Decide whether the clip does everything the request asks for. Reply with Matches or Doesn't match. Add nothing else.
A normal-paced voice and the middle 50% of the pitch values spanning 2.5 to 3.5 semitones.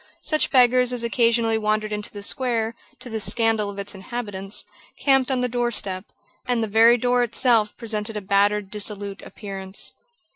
Matches